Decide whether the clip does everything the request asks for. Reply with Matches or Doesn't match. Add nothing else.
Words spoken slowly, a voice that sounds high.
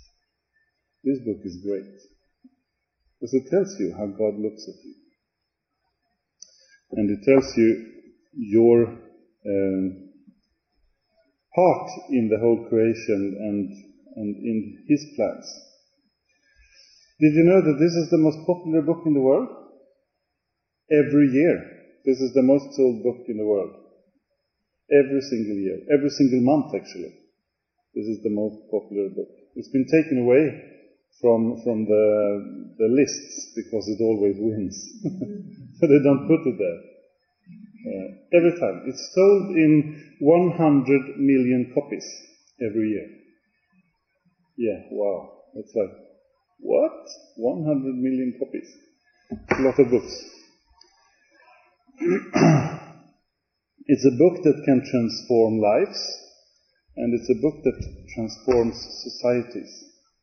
Doesn't match